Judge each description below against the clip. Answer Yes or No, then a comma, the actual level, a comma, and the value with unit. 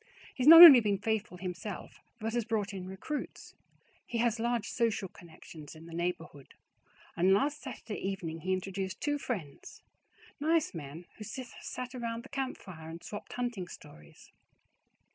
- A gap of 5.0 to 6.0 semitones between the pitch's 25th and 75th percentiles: Yes, wide, 5.5 semitones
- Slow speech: No, average, 155 wpm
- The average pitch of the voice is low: No, high, 205 Hz